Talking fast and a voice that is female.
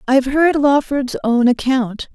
No: average, 170 wpm; female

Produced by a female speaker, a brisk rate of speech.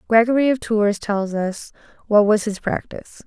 No: female; average, 165 wpm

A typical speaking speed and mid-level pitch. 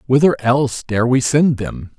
No: average, 180 wpm; low, 130 Hz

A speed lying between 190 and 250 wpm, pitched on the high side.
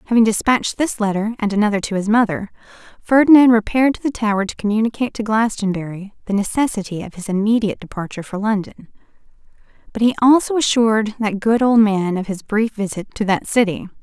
No: average, 175 wpm; high, 215 Hz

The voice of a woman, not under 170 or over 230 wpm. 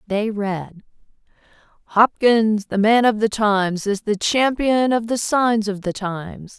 No: female; average, 155 wpm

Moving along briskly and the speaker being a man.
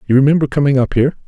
Yes: fast, 235 wpm; male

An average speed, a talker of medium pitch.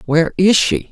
Yes: average, 195 wpm; medium, 180 Hz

